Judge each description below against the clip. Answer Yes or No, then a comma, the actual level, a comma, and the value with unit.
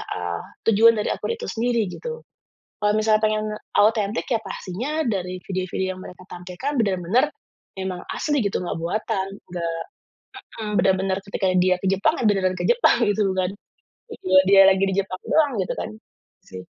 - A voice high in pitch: Yes, high, 195 Hz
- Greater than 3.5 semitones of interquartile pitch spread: No, average, 3.2 semitones